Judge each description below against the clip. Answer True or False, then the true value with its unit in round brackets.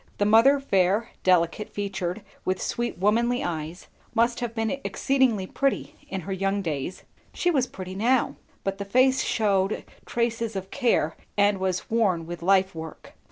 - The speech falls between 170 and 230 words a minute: False (160 wpm)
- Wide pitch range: False (4.0 semitones)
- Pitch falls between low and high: False (200 Hz)